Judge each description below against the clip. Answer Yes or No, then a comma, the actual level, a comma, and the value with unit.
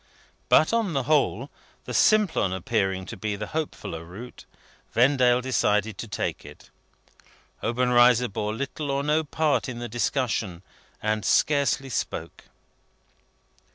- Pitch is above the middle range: No, low, 125 Hz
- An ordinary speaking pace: No, slow, 125 wpm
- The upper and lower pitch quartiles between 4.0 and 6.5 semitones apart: Yes, average, 4.9 semitones